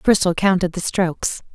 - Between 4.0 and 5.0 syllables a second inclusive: No, 5.2 syllables/s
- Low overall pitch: No, medium, 185 Hz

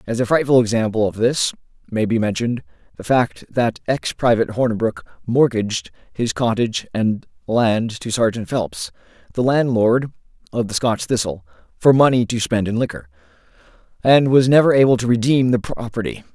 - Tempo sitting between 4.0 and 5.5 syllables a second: Yes, 5.3 syllables/s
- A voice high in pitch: No, low, 115 Hz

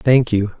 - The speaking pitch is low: Yes, low, 115 Hz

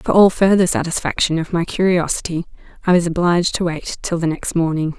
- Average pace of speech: Yes, average, 195 wpm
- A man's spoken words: No, female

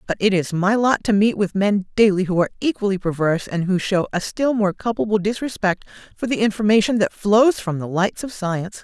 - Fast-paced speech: Yes, fast, 215 wpm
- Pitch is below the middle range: No, high, 200 Hz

